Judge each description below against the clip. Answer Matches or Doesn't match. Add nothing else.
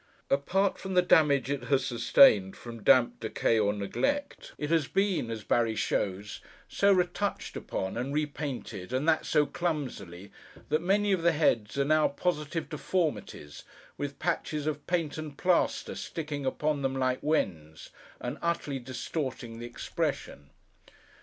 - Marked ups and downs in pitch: Matches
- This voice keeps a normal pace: Matches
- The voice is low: Doesn't match